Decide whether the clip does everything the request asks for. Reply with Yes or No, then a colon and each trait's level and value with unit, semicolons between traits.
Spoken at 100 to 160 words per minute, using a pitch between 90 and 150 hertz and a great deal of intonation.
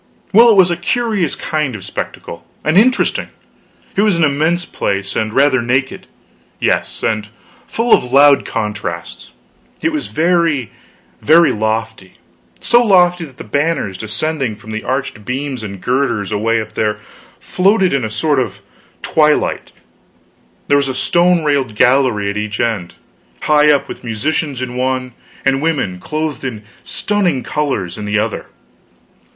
Yes: average, 155 wpm; low, 135 Hz; wide, 6.7 semitones